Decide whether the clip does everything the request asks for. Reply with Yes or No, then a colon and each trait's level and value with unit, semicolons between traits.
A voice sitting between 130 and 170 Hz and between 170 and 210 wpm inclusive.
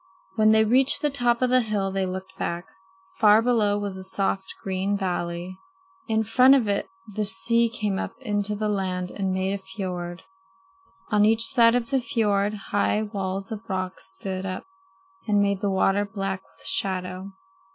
No: high, 200 Hz; average, 175 wpm